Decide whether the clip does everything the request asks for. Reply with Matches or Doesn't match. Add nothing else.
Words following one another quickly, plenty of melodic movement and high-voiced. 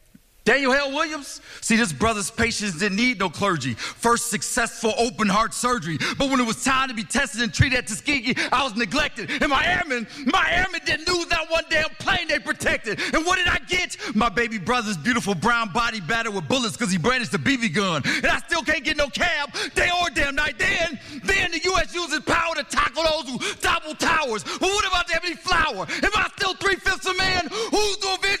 Matches